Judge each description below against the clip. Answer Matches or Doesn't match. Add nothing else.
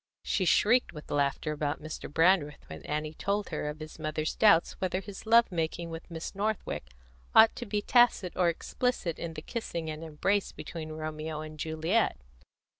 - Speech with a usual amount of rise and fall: Matches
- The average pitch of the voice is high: Doesn't match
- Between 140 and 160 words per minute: Doesn't match